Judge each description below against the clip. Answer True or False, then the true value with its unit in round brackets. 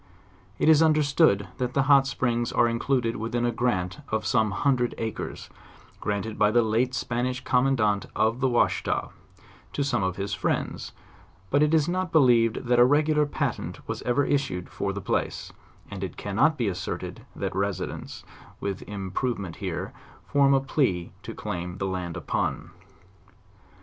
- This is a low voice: True (120 Hz)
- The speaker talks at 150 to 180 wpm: True (160 wpm)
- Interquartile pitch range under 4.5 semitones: False (5.2 semitones)